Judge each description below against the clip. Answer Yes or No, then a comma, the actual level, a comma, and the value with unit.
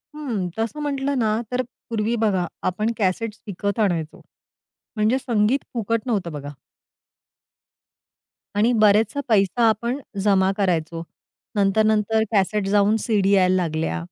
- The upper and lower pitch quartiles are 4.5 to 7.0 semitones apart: No, average, 3.1 semitones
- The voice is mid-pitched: No, high, 210 Hz